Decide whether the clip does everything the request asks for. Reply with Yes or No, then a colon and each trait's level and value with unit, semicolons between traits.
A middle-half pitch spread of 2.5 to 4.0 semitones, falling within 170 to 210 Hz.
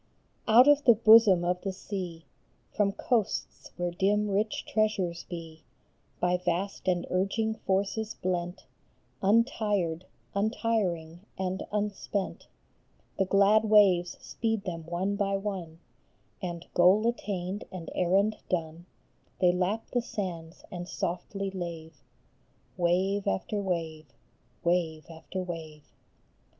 Yes: average, 3.1 semitones; medium, 185 Hz